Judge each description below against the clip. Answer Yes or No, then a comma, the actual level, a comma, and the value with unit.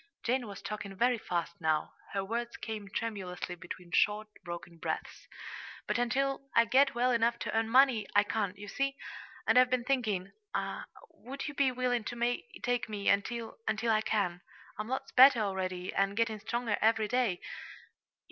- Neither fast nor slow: Yes, average, 165 wpm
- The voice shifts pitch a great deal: No, average, 3.7 semitones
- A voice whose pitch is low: No, high, 225 Hz